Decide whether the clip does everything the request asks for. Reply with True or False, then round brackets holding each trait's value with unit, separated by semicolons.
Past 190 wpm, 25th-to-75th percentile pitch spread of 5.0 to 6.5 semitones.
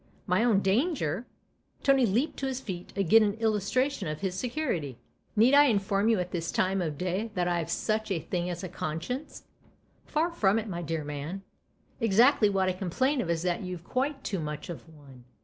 True (200 wpm; 5.3 semitones)